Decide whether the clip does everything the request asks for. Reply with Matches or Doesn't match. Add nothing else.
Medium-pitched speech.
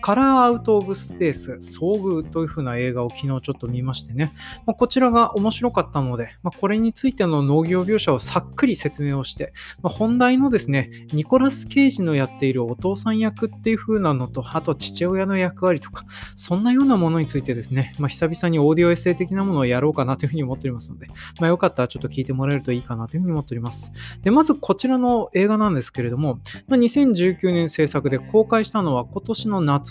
Matches